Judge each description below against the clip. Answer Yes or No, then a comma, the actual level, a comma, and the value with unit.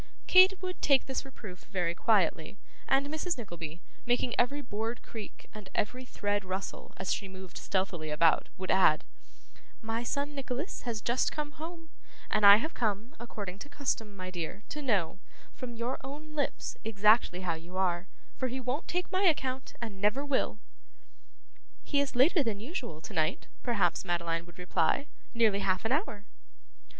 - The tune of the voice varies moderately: No, wide, 6.4 semitones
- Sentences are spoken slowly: No, average, 165 wpm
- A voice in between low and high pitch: No, high, 225 Hz